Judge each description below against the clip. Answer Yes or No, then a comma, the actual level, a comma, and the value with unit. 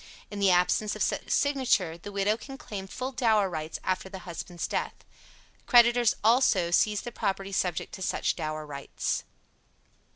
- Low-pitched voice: No, high, 195 Hz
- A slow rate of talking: No, average, 160 wpm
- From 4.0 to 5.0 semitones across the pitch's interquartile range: Yes, average, 4.7 semitones